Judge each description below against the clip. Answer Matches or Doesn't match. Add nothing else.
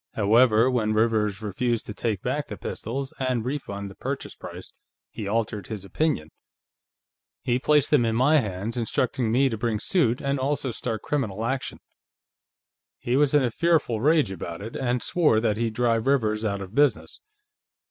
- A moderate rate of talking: Matches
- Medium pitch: Doesn't match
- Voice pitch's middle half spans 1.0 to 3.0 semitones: Doesn't match